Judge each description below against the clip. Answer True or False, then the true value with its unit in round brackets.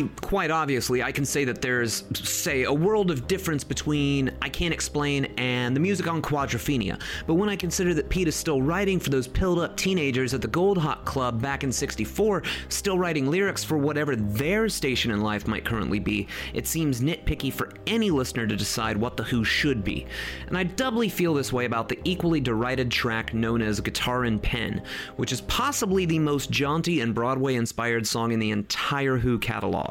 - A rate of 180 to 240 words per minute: True (200 wpm)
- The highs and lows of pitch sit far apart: True (6.1 semitones)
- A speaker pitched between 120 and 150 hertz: True (135 Hz)